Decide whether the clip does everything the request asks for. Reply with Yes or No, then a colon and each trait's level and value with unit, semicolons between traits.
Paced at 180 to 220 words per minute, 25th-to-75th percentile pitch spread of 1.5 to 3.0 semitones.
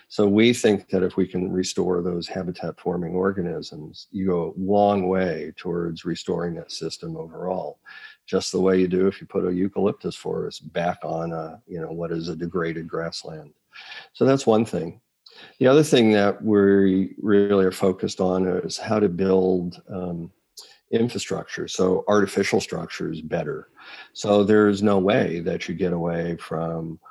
No: average, 165 wpm; average, 2.7 semitones